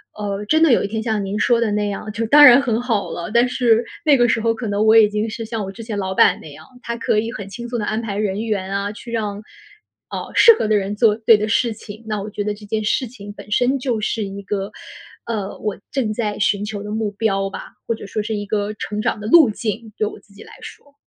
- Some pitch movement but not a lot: No, narrow, 1.9 semitones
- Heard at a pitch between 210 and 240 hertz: Yes, high, 215 Hz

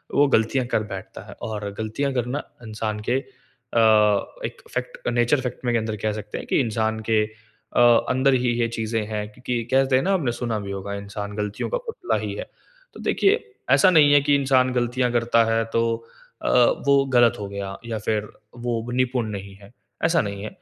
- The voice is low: Yes, low, 115 Hz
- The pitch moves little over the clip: No, average, 3.2 semitones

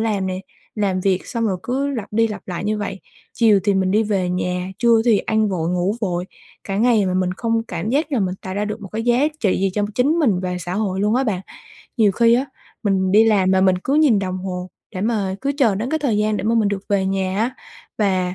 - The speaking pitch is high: Yes, high, 205 Hz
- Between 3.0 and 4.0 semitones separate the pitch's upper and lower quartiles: Yes, average, 3.3 semitones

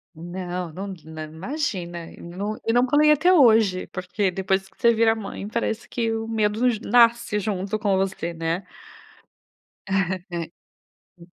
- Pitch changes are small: No, average, 4.1 semitones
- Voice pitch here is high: Yes, high, 200 Hz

